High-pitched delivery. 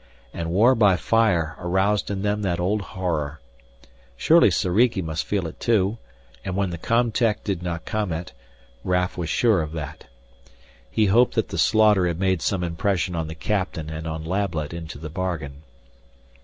No: very low, 90 Hz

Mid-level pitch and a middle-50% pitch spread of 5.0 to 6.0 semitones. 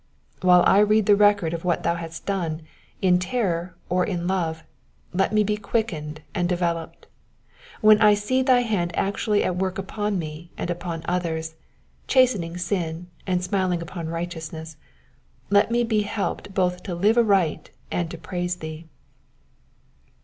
No: medium, 180 Hz; average, 3.4 semitones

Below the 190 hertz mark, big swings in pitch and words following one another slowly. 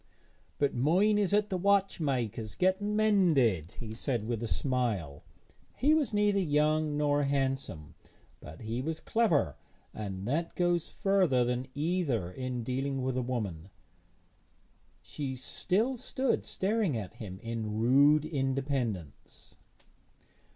Yes: low, 135 Hz; wide, 7.7 semitones; slow, 125 wpm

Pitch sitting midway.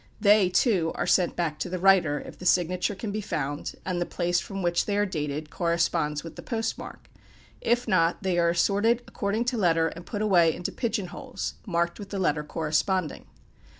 Yes: medium, 180 Hz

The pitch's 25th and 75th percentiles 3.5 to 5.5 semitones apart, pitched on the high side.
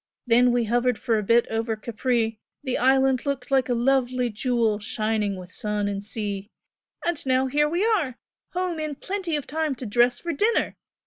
Yes: average, 3.9 semitones; high, 245 Hz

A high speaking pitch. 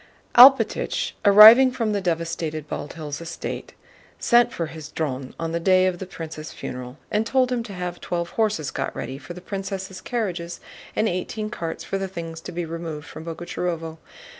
No: medium, 175 Hz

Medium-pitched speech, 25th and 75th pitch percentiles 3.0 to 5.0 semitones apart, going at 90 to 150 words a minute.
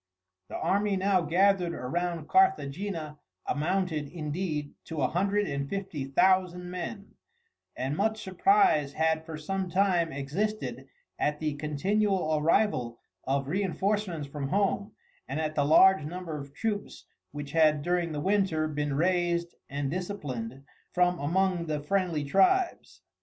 Yes: medium, 170 Hz; average, 4.6 semitones; slow, 135 wpm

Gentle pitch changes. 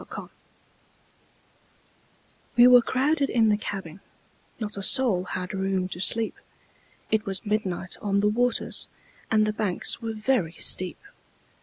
No: average, 3.4 semitones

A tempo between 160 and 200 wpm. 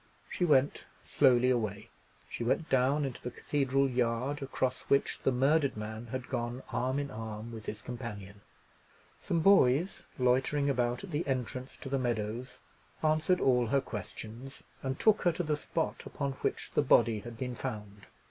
Yes: average, 165 wpm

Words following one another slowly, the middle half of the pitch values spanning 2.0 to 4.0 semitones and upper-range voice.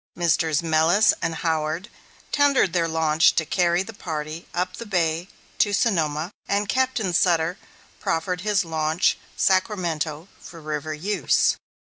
No: slow, 130 wpm; average, 3.2 semitones; medium, 170 Hz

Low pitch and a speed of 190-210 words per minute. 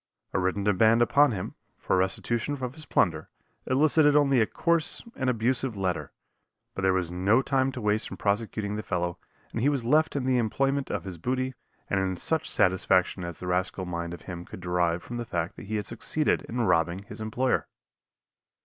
Yes: low, 110 Hz; average, 195 wpm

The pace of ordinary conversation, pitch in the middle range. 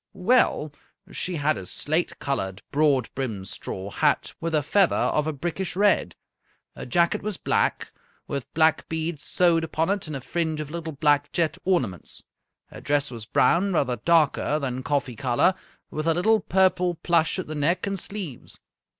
Yes: average, 170 wpm; medium, 155 Hz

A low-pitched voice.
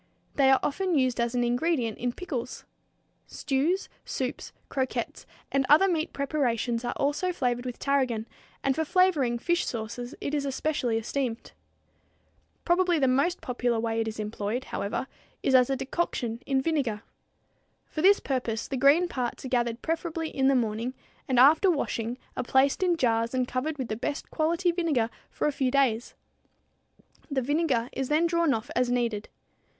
No: very high, 265 Hz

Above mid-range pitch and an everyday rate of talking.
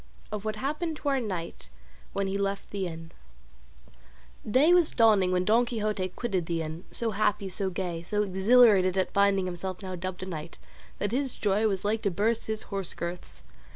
Yes: high, 200 Hz; average, 190 wpm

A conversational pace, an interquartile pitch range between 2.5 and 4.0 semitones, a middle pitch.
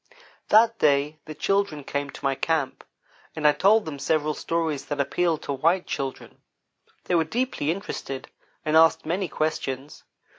Yes: average, 155 wpm; average, 3.5 semitones; medium, 155 Hz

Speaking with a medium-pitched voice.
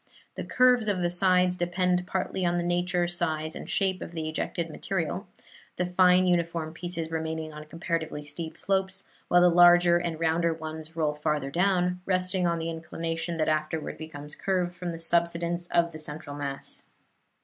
Yes: medium, 170 Hz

